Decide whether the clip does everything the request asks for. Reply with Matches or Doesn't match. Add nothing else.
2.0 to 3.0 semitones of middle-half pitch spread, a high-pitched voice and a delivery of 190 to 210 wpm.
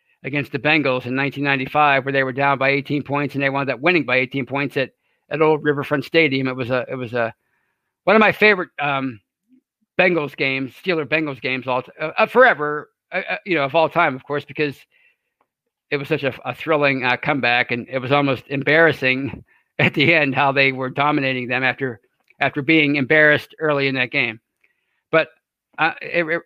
Doesn't match